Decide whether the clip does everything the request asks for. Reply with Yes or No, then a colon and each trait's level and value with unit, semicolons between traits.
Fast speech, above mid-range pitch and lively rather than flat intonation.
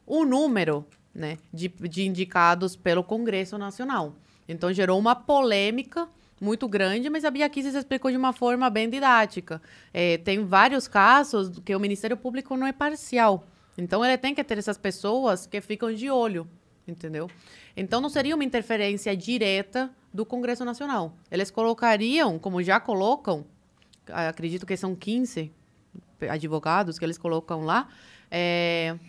No: average, 145 wpm; high, 205 Hz; wide, 5.9 semitones